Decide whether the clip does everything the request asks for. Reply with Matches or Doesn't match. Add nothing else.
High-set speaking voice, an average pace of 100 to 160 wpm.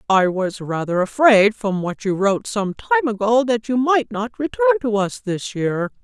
Doesn't match